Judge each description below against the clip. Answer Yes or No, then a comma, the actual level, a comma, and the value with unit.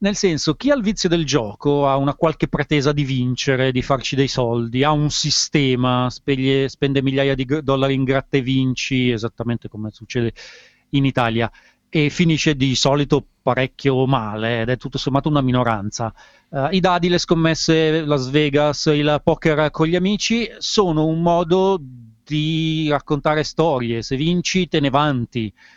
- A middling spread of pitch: Yes, average, 3.7 semitones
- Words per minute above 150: Yes, average, 165 wpm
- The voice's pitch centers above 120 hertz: Yes, medium, 140 Hz